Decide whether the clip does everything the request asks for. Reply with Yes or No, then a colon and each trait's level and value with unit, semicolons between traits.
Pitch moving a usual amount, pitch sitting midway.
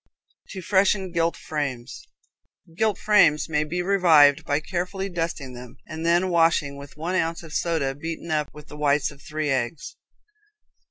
Yes: average, 3.3 semitones; medium, 160 Hz